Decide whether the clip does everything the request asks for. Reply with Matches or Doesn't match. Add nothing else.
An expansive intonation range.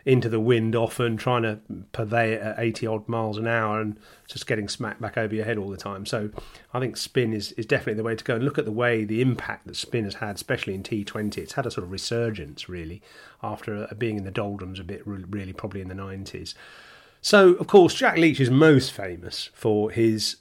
Doesn't match